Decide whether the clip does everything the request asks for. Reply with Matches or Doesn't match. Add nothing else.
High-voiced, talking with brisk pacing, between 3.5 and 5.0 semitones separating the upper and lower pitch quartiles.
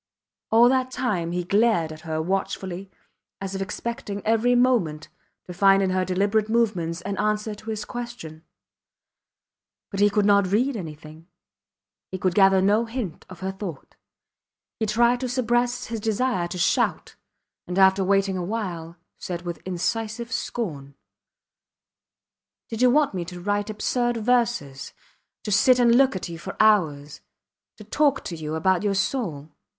Doesn't match